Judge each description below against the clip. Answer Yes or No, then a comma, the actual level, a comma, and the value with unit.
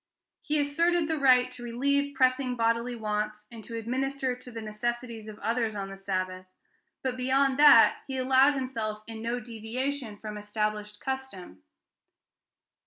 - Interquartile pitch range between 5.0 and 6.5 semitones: No, average, 3.7 semitones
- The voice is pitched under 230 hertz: No, high, 240 Hz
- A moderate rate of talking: Yes, average, 150 wpm